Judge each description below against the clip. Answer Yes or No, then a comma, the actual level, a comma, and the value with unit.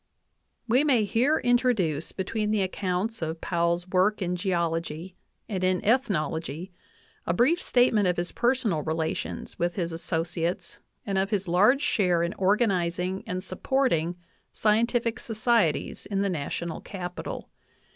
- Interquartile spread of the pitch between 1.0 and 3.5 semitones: No, average, 4.5 semitones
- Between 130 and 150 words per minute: Yes, slow, 135 wpm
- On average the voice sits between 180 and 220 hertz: Yes, medium, 185 Hz